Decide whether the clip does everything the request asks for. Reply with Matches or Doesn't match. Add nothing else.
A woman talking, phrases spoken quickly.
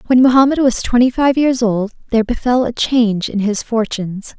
Doesn't match